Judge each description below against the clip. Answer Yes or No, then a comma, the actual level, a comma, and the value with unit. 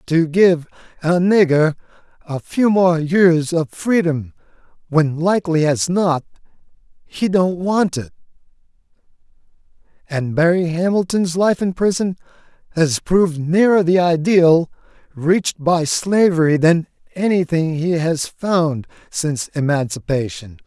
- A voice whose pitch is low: No, medium, 170 Hz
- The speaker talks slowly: Yes, slow, 115 wpm